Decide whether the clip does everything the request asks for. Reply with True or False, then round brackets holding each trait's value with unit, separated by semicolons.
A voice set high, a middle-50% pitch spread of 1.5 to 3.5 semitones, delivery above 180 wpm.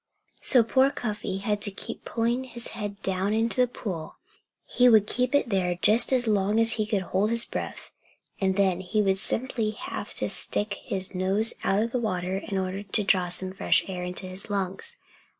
True (205 Hz; 3.2 semitones; 200 wpm)